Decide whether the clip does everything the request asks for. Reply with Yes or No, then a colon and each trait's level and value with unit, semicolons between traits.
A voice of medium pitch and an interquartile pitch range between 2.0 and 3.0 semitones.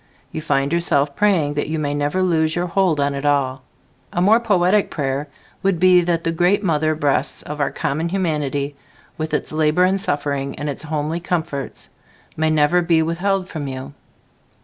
No: medium, 155 Hz; average, 3.5 semitones